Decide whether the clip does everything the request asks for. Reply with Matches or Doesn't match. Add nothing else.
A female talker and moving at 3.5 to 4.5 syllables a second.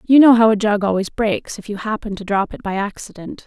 Doesn't match